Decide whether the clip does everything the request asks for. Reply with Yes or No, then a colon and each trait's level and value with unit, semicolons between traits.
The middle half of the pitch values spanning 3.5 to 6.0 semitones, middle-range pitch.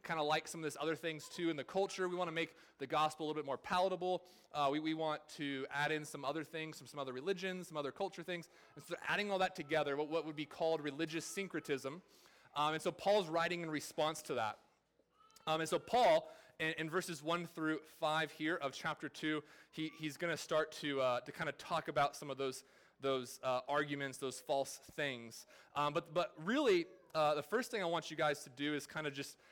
No: average, 2.7 semitones; medium, 155 Hz